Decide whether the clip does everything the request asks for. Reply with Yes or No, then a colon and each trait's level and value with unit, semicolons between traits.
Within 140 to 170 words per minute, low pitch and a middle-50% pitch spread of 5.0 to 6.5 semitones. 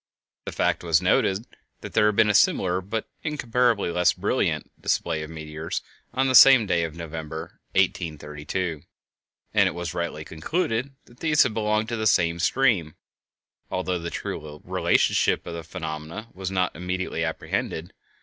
Yes: average, 160 wpm; very low, 90 Hz; average, 5.3 semitones